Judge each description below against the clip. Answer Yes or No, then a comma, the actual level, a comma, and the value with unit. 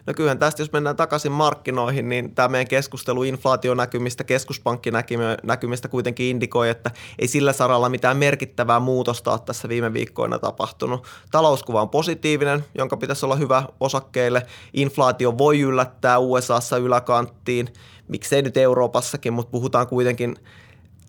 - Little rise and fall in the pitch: Yes, narrow, 1.9 semitones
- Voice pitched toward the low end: Yes, low, 125 Hz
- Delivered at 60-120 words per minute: No, average, 130 wpm